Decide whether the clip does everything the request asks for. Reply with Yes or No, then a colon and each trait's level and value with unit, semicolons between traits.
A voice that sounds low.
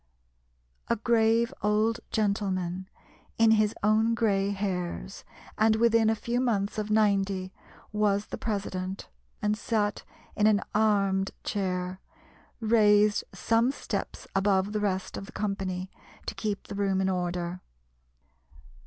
No: high, 205 Hz